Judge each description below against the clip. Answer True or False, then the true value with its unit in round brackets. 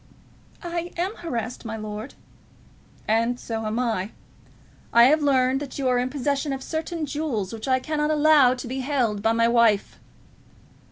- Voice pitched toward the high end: True (255 Hz)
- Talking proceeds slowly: False (165 wpm)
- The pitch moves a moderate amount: True (4.5 semitones)